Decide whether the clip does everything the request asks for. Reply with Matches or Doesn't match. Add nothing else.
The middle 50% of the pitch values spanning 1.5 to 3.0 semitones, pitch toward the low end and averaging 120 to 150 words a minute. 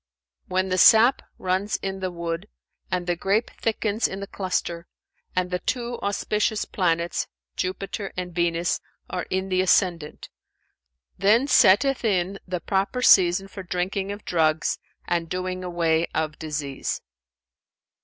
Doesn't match